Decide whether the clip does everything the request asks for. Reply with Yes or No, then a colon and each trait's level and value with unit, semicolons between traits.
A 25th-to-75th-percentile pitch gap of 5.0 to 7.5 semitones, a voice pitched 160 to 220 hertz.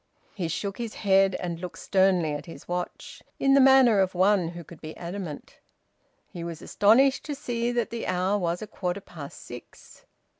No: average, 4.2 semitones; high, 190 Hz